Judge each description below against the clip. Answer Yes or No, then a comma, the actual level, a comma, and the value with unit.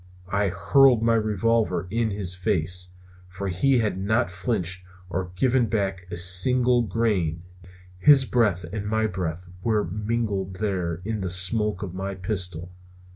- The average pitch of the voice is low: Yes, low, 100 Hz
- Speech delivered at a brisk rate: No, average, 145 wpm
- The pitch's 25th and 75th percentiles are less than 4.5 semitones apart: Yes, average, 3.8 semitones